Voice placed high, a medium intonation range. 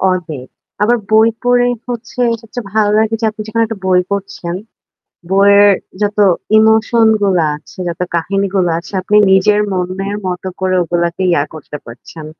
Yes: high, 195 Hz; average, 3.4 semitones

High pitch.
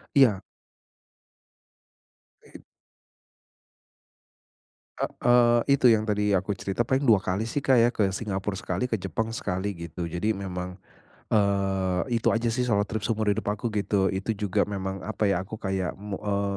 No: low, 100 Hz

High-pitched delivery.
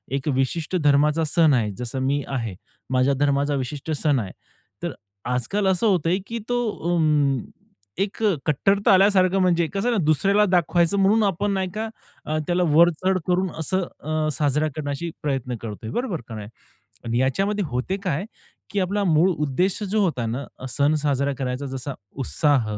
No: medium, 155 Hz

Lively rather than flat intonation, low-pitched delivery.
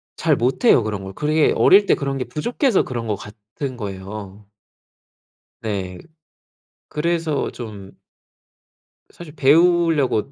Yes: wide, 6.9 semitones; low, 130 Hz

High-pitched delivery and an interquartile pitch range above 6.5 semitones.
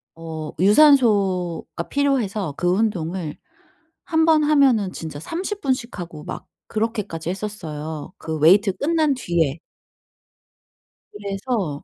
Yes: high, 195 Hz; wide, 7.6 semitones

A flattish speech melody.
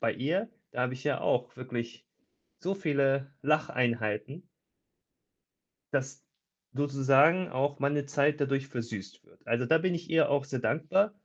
No: average, 3.3 semitones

